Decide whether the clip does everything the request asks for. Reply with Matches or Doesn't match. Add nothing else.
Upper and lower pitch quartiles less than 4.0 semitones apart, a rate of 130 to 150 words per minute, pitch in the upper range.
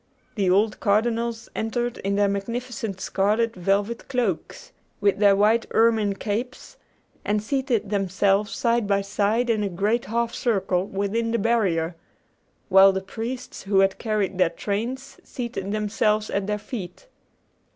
Matches